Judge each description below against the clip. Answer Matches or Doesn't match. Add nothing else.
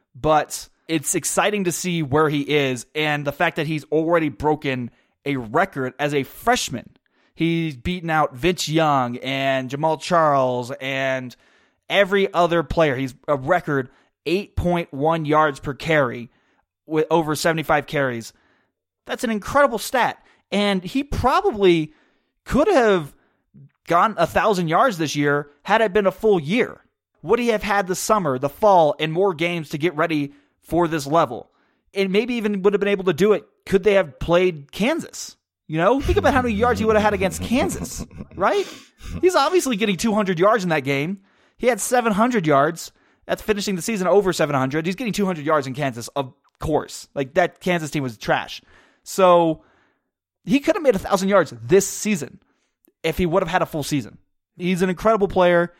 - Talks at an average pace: Matches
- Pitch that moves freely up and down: Matches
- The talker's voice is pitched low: Doesn't match